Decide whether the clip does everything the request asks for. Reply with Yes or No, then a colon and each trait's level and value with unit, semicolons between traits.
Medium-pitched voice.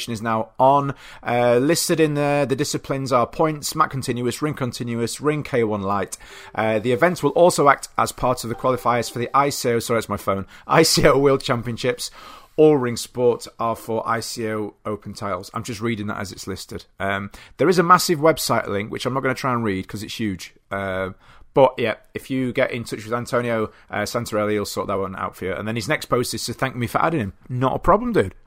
No: low, 120 Hz